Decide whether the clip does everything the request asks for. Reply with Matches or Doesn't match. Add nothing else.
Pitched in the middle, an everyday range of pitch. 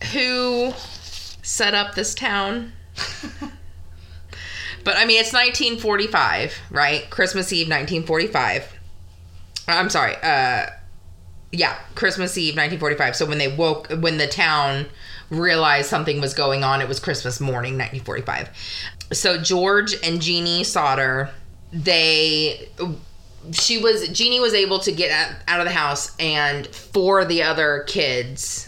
Doesn't match